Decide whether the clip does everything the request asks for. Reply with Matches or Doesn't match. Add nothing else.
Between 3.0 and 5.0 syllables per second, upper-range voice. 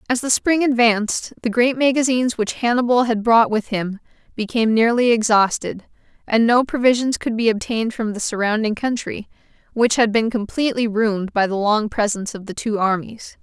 Doesn't match